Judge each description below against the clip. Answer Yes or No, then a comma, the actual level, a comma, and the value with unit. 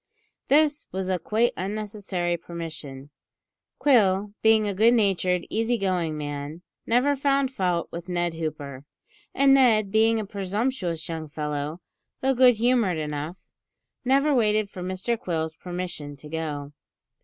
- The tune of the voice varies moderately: No, wide, 5.8 semitones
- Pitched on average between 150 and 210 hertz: Yes, medium, 185 Hz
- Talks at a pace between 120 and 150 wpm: Yes, slow, 135 wpm